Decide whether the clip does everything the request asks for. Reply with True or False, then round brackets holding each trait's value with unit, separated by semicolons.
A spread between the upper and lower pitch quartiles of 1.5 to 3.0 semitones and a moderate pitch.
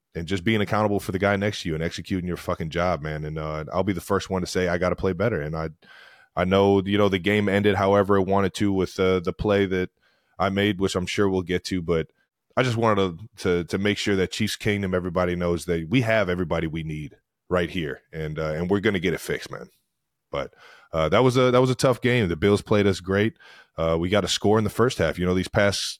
False (2.7 semitones; 95 Hz)